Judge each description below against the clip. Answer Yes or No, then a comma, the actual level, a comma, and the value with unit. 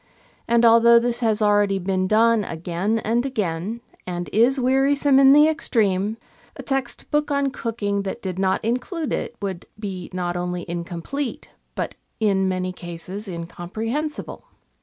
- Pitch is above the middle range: Yes, high, 215 Hz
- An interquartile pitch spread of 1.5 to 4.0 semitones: No, average, 5.0 semitones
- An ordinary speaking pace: Yes, average, 145 wpm